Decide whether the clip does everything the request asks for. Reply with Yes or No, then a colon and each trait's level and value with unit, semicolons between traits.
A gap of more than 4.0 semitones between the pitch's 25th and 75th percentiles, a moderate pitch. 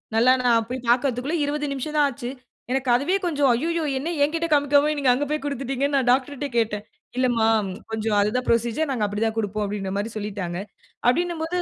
No: average, 4.5 semitones; very high, 255 Hz